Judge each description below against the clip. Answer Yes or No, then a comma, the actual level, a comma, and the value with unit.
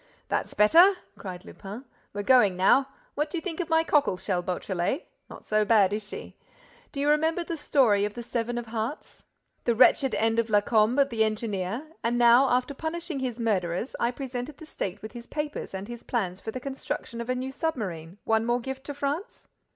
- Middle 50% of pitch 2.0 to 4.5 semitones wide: No, average, 5.0 semitones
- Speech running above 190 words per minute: Yes, average, 200 wpm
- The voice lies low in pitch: No, high, 240 Hz